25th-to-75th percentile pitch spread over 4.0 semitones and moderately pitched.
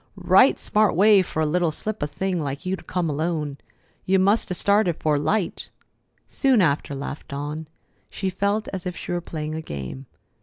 Yes: average, 4.4 semitones; medium, 170 Hz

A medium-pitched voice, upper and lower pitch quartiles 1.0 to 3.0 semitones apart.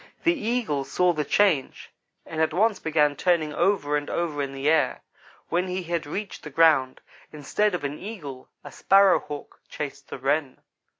No: medium, 160 Hz; average, 4.3 semitones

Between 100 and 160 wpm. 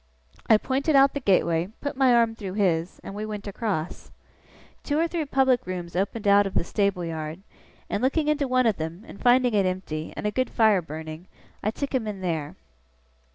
No: average, 200 wpm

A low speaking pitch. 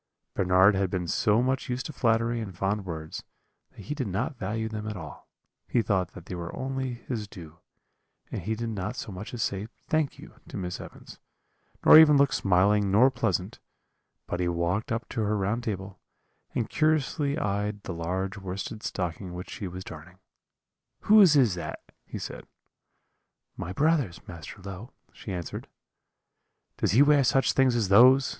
Yes: low, 105 Hz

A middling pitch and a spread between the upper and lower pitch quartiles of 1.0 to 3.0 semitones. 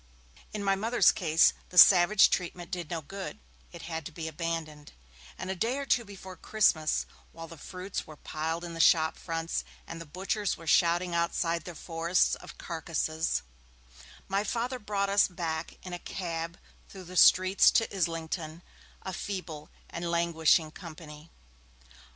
Yes: medium, 170 Hz; average, 2.7 semitones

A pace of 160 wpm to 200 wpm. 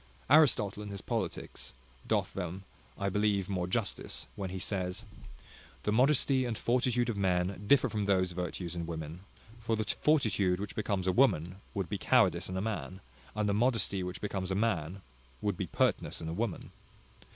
Yes: average, 175 wpm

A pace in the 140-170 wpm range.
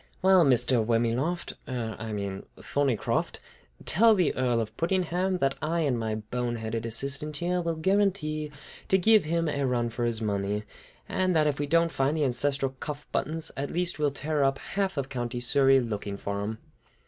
No: average, 185 wpm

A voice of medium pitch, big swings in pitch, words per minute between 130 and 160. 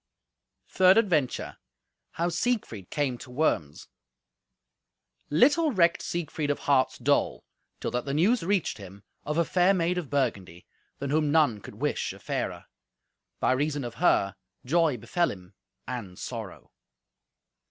Yes: medium, 145 Hz; wide, 6.0 semitones; average, 140 wpm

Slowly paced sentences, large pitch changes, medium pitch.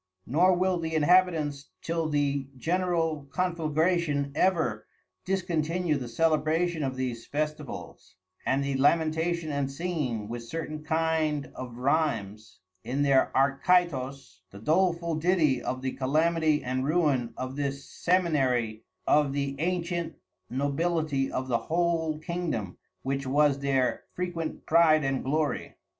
No: slow, 125 wpm; average, 3.8 semitones; medium, 150 Hz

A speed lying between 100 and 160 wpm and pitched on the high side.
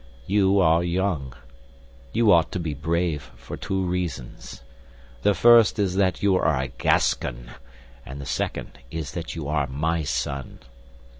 No: average, 150 wpm; very low, 85 Hz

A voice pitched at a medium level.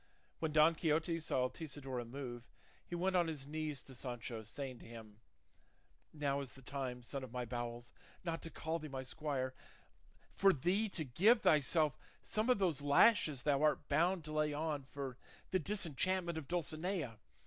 Yes: medium, 150 Hz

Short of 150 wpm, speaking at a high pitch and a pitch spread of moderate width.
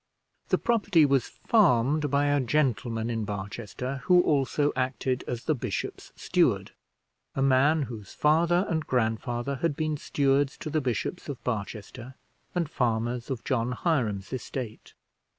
No: average, 140 wpm; low, 130 Hz; average, 4.2 semitones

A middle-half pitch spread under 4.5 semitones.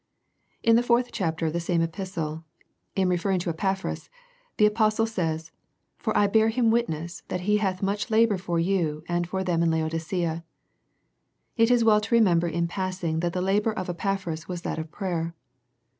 Yes: average, 4.0 semitones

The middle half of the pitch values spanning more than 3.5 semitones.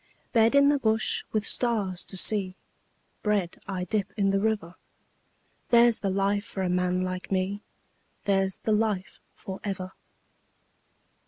No: average, 2.7 semitones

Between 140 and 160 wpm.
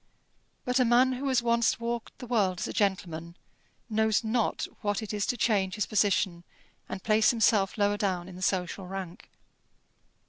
No: average, 175 wpm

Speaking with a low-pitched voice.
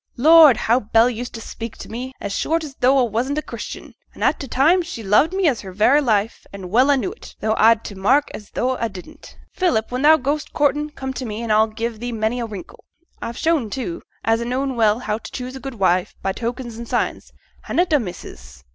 No: high, 240 Hz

